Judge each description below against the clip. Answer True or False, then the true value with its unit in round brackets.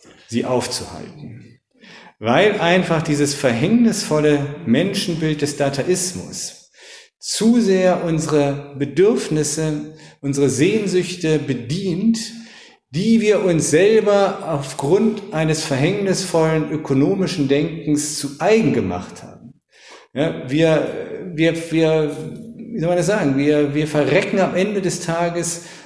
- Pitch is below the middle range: False (165 Hz)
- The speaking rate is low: True (105 wpm)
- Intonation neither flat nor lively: True (4.7 semitones)